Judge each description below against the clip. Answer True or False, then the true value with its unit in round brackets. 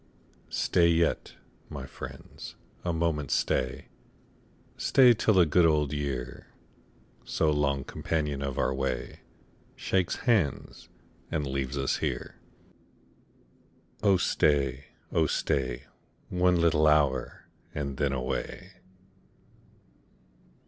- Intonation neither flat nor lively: True (3.6 semitones)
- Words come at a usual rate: False (105 wpm)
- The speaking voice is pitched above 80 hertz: False (75 Hz)